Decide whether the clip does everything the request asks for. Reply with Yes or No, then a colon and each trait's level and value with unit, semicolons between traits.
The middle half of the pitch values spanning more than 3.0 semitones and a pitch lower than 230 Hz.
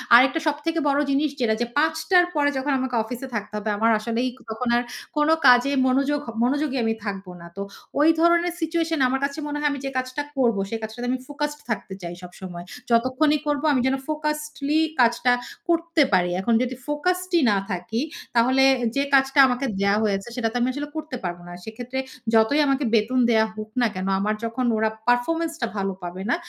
No: average, 4.9 semitones; very high, 255 Hz